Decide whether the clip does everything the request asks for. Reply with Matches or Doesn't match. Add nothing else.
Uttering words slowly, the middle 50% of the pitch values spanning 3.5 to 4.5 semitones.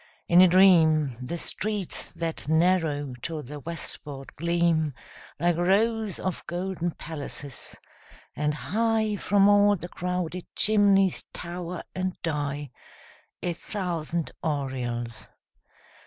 Matches